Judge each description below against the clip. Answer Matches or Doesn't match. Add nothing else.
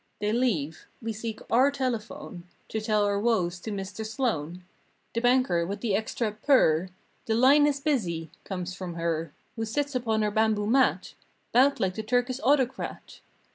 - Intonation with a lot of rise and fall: Doesn't match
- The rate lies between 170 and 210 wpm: Matches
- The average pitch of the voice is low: Doesn't match